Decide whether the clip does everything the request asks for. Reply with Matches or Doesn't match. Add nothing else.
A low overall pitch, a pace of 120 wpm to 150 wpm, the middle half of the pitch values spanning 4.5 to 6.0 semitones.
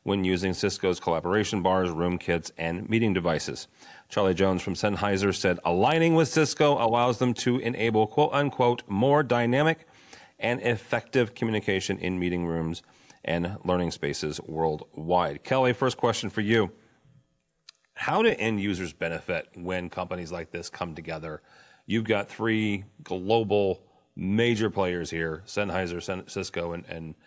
Matches